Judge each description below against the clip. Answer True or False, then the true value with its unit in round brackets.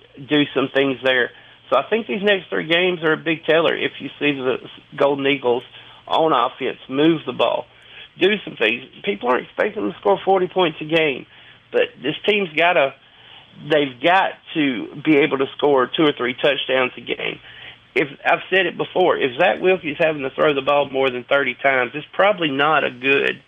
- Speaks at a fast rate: False (195 wpm)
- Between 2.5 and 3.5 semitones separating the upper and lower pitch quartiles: False (5.0 semitones)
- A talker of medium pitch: True (150 Hz)